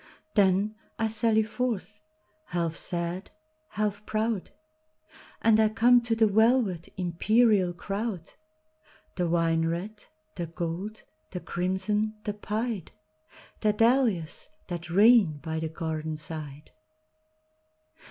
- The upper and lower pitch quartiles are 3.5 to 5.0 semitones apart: Yes, average, 4.6 semitones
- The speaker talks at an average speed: No, slow, 100 wpm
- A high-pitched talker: Yes, high, 210 Hz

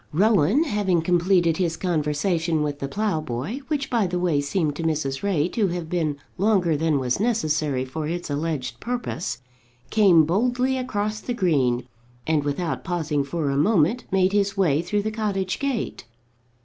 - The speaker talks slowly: No, average, 160 wpm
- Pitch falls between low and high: Yes, medium, 175 Hz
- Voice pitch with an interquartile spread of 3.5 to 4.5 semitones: No, wide, 5.4 semitones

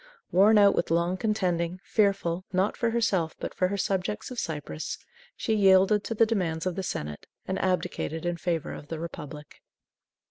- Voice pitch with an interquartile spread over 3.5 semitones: No, average, 3.2 semitones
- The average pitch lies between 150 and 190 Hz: Yes, medium, 185 Hz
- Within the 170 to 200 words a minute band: Yes, average, 175 wpm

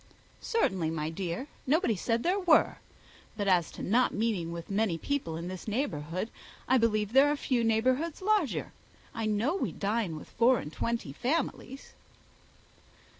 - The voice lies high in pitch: Yes, high, 225 Hz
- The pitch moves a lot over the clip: Yes, wide, 6.6 semitones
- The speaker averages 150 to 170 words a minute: Yes, average, 155 wpm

